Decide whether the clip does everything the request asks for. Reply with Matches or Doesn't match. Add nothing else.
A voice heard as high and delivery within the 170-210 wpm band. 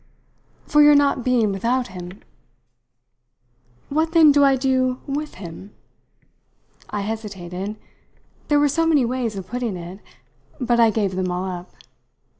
Doesn't match